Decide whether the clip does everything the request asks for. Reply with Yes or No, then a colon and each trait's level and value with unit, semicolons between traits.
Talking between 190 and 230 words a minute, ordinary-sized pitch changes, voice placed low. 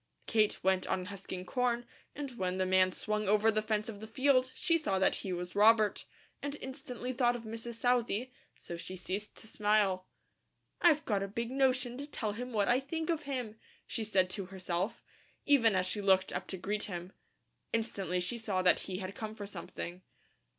No: average, 195 wpm; average, 4.4 semitones; high, 215 Hz